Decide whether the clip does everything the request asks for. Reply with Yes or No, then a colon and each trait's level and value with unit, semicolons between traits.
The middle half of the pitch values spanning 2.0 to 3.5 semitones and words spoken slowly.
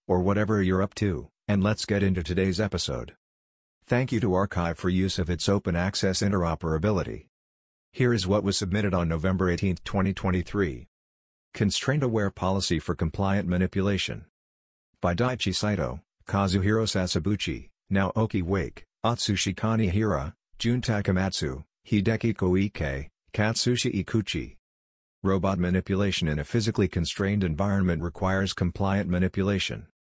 Yes: average, 2.9 semitones; slow, 125 wpm